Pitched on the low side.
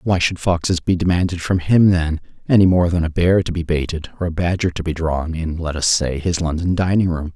Yes: very low, 85 Hz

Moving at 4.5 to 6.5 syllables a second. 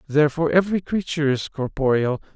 No: 6.8 syllables/s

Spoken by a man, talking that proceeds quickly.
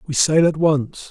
Yes: male; fast, 215 wpm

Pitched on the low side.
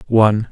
Yes: low, 110 Hz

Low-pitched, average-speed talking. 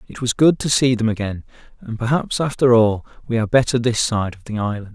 No: low, 115 Hz; fast, 230 wpm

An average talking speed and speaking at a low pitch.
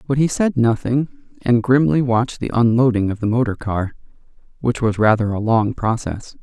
Yes: average, 175 wpm; low, 120 Hz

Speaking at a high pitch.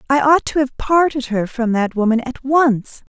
Yes: very high, 260 Hz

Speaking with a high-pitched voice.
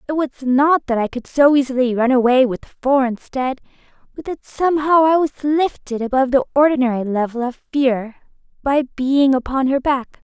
Yes: very high, 265 Hz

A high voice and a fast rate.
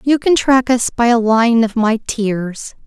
Yes: high, 235 Hz; fast, 210 wpm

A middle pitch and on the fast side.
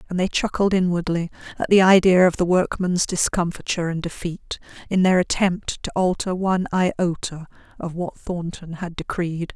No: medium, 180 Hz; average, 155 wpm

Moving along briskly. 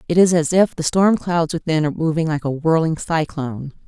Yes: fast, 215 wpm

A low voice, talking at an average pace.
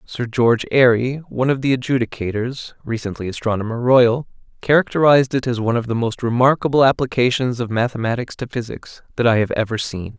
Yes: low, 120 Hz; average, 165 wpm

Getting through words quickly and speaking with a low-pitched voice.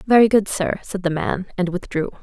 No: fast, 215 wpm; high, 190 Hz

